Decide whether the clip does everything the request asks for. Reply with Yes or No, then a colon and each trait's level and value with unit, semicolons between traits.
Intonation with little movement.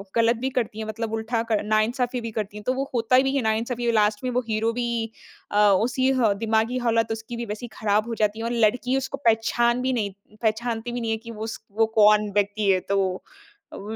Yes: narrow, 1.9 semitones